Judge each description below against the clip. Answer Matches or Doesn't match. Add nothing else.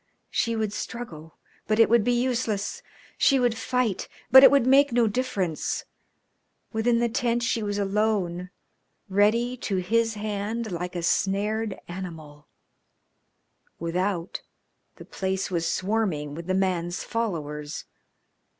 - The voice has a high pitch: Matches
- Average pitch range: Matches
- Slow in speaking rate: Matches